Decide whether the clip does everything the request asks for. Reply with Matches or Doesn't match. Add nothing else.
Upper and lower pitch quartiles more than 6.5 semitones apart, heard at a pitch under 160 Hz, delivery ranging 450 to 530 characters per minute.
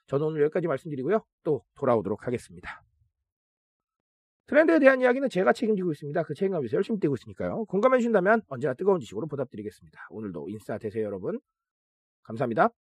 Doesn't match